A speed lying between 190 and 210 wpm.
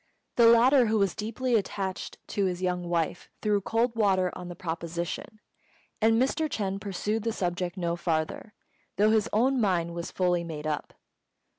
No: average, 165 wpm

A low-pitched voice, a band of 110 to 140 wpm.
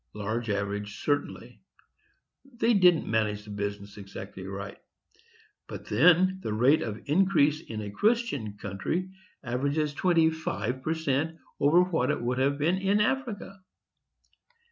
No: medium, 145 Hz; slow, 135 wpm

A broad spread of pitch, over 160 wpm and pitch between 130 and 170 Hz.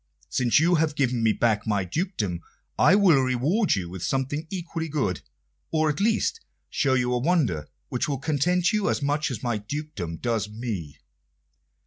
Yes: wide, 6.7 semitones; average, 170 wpm; low, 135 Hz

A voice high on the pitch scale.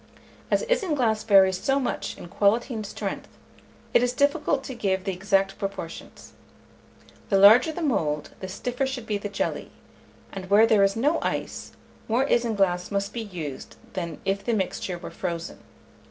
Yes: high, 205 Hz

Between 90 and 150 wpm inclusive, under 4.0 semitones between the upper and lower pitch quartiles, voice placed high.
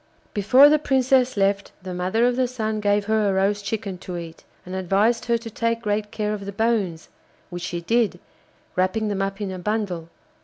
No: average, 200 wpm; average, 3.3 semitones; high, 205 Hz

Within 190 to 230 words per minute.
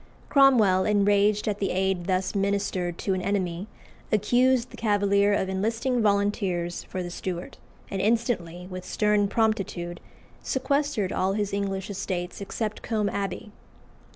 No: slow, 135 wpm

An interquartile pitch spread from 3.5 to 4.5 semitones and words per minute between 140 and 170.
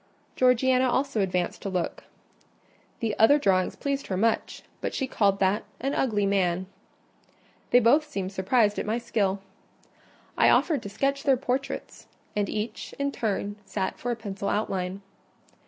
No: average, 4.9 semitones; average, 155 wpm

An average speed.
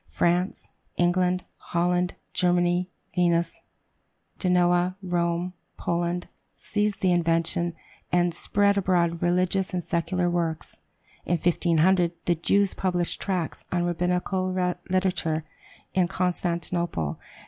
No: slow, 100 wpm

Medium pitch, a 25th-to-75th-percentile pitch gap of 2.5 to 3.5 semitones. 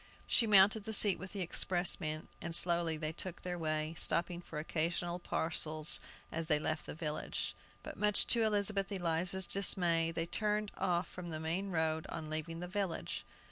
Yes: medium, 170 Hz; average, 3.1 semitones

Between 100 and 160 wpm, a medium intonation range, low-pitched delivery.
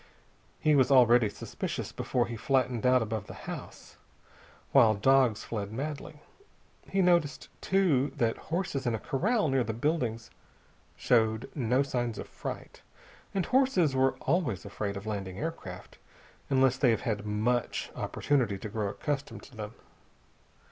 Yes: average, 145 wpm; average, 4.6 semitones; low, 125 Hz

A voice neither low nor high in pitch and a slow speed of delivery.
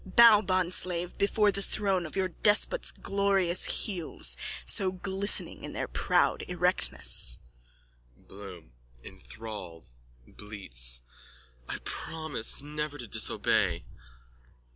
Yes: medium, 170 Hz; slow, 100 wpm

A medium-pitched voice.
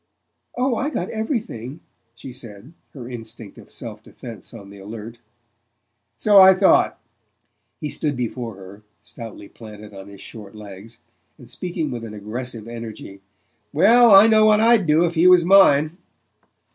No: low, 125 Hz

